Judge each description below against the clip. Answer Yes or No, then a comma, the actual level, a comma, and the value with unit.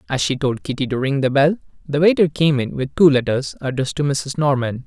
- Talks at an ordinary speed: No, fast, 235 wpm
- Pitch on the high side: No, medium, 140 Hz